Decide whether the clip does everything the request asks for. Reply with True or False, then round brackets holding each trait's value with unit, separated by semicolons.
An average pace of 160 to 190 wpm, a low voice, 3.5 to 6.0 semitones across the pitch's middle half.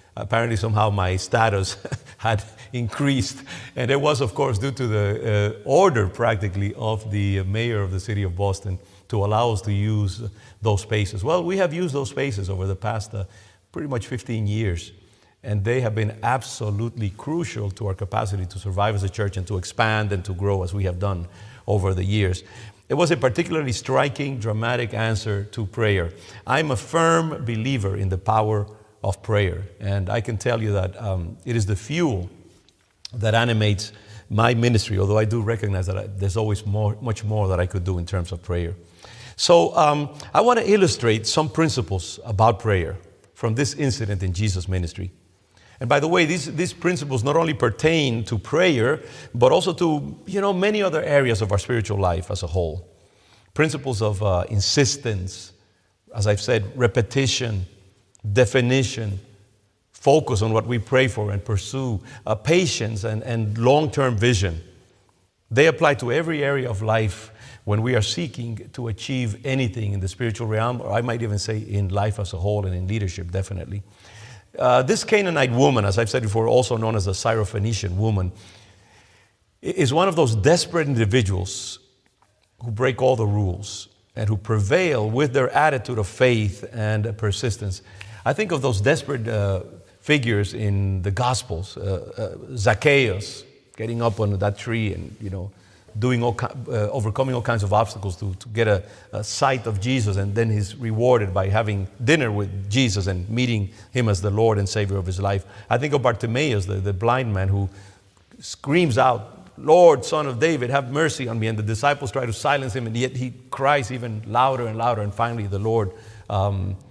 True (180 wpm; 110 Hz; 3.8 semitones)